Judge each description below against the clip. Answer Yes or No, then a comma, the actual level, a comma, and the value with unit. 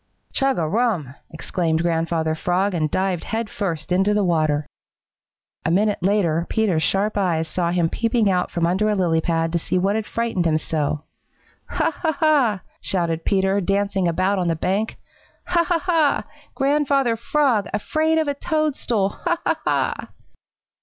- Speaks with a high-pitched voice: Yes, high, 195 Hz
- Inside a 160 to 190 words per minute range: Yes, average, 165 wpm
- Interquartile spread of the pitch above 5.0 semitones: Yes, wide, 5.4 semitones